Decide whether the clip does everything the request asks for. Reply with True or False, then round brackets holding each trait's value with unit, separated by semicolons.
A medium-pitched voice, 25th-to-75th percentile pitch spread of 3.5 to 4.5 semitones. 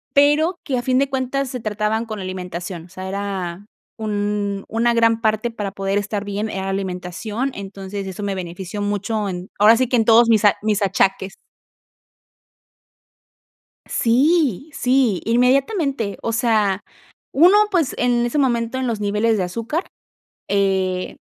False (215 Hz; 3.8 semitones)